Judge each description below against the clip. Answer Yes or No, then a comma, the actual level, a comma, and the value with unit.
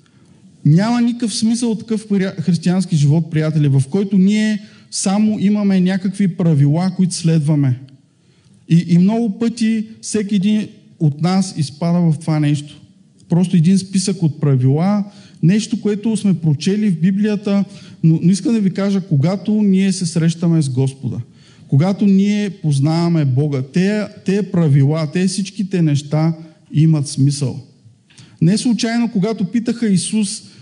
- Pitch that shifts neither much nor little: Yes, average, 4.7 semitones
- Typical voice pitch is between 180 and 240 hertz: Yes, medium, 185 Hz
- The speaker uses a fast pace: No, average, 135 wpm